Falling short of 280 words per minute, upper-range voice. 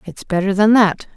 Yes: fast, 205 wpm; high, 200 Hz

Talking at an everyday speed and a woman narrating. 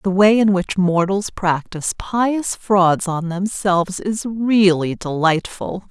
No: slow, 130 wpm; female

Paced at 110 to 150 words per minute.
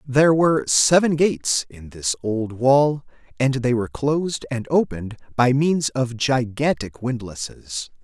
Yes: average, 140 wpm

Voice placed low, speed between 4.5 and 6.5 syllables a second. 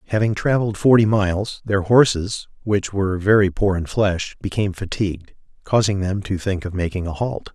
Yes: low, 100 Hz; 5.3 syllables/s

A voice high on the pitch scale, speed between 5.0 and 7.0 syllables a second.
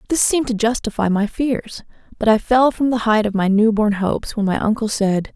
Yes: high, 220 Hz; 5.5 syllables/s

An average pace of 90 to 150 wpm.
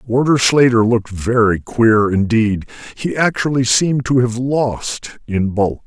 Yes: slow, 135 wpm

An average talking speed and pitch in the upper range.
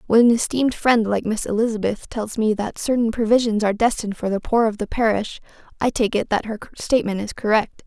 No: fast, 215 wpm; high, 220 Hz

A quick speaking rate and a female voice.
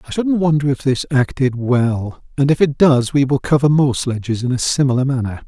No: fast, 220 wpm; male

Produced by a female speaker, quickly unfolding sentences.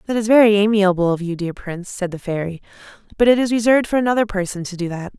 Yes: female; fast, 245 wpm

